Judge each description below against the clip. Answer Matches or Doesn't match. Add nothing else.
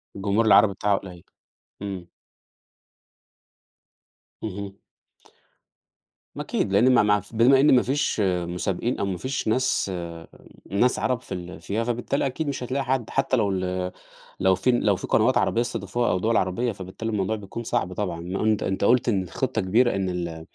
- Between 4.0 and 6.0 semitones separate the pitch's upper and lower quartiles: Matches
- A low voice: Matches